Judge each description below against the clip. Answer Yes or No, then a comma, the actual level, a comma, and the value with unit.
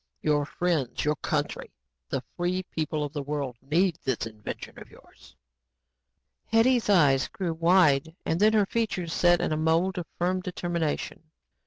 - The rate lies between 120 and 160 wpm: Yes, average, 155 wpm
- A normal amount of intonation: Yes, average, 3.6 semitones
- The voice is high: No, medium, 165 Hz